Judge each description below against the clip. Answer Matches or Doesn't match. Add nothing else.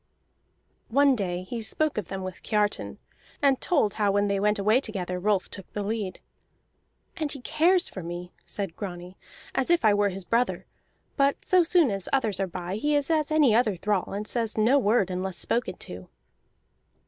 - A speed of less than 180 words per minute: Doesn't match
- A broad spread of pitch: Matches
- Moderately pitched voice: Doesn't match